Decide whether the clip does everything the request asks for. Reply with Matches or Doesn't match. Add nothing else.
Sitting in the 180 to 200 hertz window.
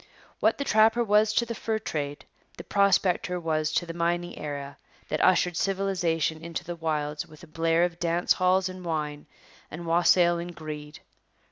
Doesn't match